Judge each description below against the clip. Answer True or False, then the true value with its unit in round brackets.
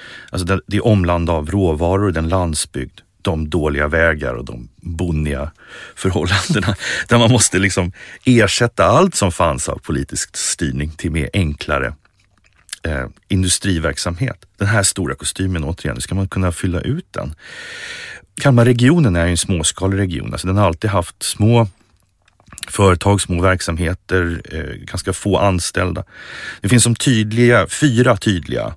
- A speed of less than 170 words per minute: True (140 wpm)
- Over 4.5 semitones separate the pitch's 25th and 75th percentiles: False (4.2 semitones)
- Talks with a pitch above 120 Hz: False (95 Hz)